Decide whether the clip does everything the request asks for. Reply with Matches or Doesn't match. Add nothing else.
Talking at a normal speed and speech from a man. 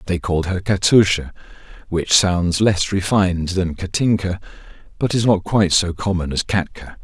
Matches